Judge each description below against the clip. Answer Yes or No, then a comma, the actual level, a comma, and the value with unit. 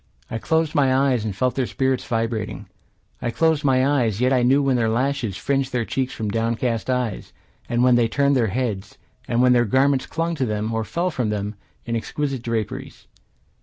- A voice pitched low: Yes, low, 125 Hz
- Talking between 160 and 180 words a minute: No, average, 200 wpm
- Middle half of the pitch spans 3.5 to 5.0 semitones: No, average, 3.1 semitones